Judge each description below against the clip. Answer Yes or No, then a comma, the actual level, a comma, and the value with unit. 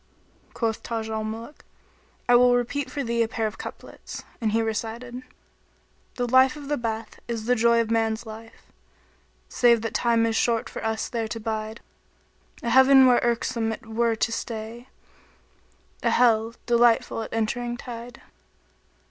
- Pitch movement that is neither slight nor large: No, narrow, 1.4 semitones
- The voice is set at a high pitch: Yes, high, 230 Hz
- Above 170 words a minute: No, average, 165 wpm